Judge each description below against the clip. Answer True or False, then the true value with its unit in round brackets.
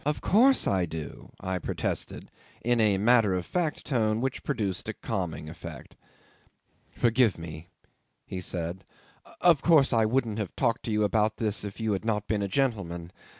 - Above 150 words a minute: True (175 wpm)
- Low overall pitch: True (105 Hz)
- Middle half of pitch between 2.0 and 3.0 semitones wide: False (4.5 semitones)